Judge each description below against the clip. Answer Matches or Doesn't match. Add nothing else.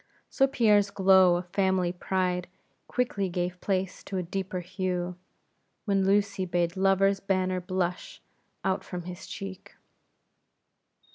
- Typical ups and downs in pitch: Doesn't match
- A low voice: Doesn't match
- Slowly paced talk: Matches